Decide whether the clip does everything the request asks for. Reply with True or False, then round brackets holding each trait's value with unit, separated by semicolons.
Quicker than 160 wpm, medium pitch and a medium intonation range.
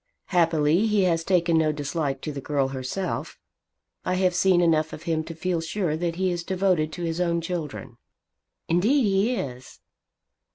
True (170 wpm; 170 Hz; 3.1 semitones)